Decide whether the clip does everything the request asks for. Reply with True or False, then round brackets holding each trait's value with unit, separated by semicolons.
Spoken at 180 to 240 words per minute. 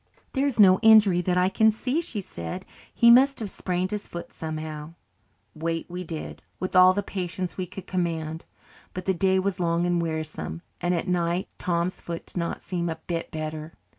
True (195 wpm)